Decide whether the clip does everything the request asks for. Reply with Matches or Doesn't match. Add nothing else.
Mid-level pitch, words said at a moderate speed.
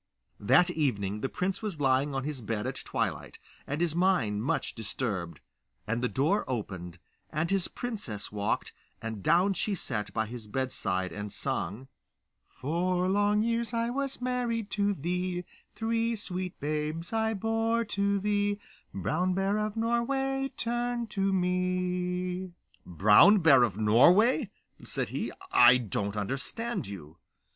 Matches